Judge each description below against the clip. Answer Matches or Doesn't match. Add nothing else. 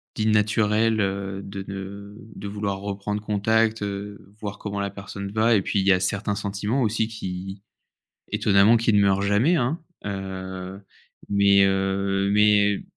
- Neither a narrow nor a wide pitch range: Doesn't match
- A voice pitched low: Matches